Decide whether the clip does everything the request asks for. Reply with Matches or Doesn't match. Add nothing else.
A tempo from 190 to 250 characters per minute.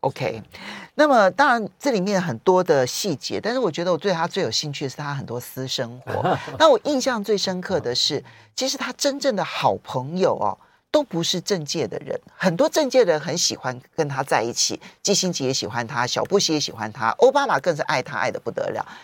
Doesn't match